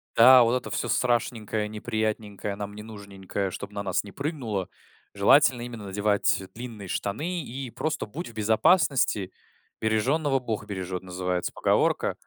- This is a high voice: No, low, 110 Hz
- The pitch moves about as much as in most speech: Yes, average, 3.6 semitones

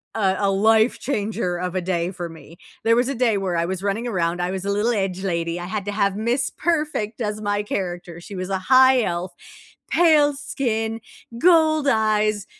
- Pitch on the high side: Yes, high, 205 Hz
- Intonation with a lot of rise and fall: No, average, 4.3 semitones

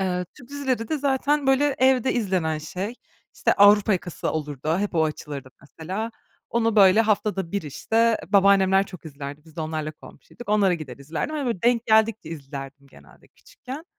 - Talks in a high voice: Yes, high, 195 Hz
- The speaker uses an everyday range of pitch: No, wide, 6.6 semitones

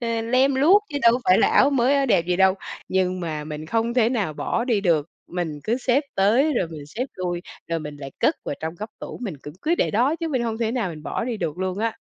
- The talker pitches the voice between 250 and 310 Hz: No, high, 215 Hz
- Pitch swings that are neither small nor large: No, wide, 6.5 semitones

